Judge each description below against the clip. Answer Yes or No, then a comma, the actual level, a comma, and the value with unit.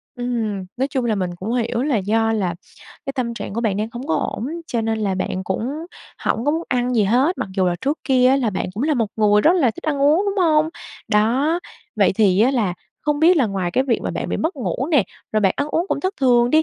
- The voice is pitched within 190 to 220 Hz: No, high, 240 Hz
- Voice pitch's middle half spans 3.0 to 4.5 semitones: No, average, 5.2 semitones